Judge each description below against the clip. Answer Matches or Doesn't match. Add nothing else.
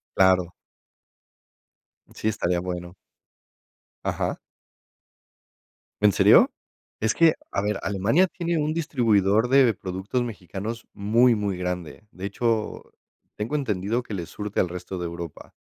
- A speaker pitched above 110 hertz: Doesn't match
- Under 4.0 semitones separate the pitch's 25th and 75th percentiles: Doesn't match